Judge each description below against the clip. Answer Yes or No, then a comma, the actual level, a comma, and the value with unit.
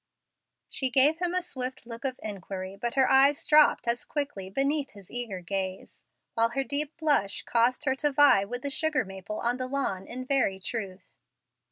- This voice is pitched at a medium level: No, very high, 255 Hz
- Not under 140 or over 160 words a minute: No, average, 185 wpm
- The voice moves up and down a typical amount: No, wide, 6.0 semitones